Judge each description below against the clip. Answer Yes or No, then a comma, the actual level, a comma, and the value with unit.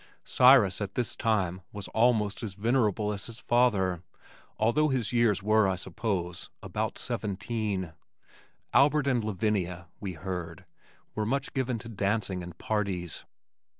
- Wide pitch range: No, average, 3.9 semitones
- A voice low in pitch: Yes, low, 105 Hz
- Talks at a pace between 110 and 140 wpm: Yes, slow, 135 wpm